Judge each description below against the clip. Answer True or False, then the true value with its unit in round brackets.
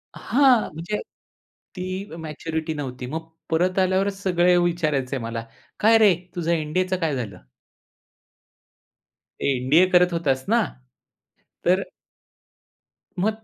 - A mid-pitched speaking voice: True (170 Hz)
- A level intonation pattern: False (3.7 semitones)